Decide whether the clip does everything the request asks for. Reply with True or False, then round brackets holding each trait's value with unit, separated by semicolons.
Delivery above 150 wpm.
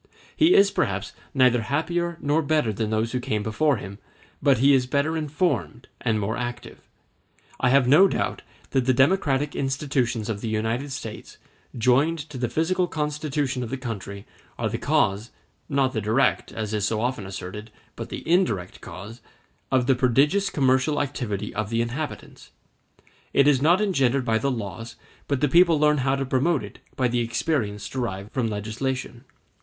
True (170 wpm)